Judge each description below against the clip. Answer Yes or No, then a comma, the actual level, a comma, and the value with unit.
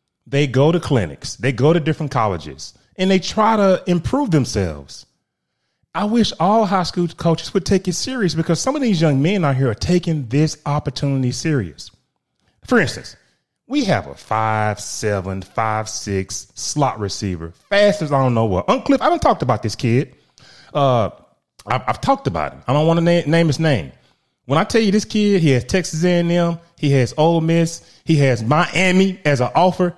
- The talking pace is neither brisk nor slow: Yes, average, 185 wpm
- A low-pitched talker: No, medium, 155 Hz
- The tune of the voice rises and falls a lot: Yes, wide, 6.5 semitones